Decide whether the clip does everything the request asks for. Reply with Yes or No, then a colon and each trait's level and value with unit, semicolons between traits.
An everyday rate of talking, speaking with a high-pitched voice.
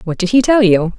No: fast, 305 wpm; high, 205 Hz